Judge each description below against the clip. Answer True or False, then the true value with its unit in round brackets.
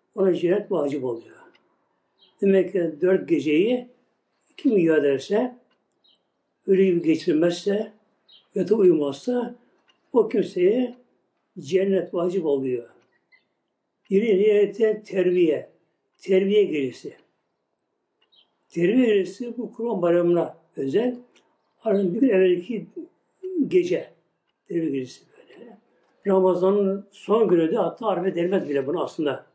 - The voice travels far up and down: False (4.7 semitones)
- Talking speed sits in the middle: True (105 wpm)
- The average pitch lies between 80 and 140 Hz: False (195 Hz)